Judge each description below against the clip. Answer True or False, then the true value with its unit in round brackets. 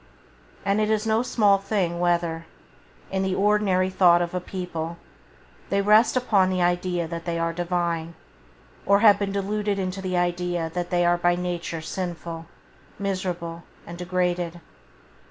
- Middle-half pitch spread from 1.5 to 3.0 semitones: True (2.4 semitones)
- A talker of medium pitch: True (180 Hz)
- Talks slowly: False (155 wpm)